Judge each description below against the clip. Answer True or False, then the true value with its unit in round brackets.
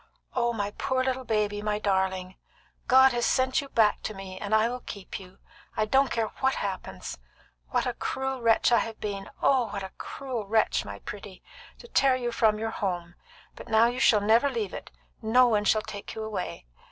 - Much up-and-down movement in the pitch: False (3.7 semitones)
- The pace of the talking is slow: False (200 wpm)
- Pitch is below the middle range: False (220 Hz)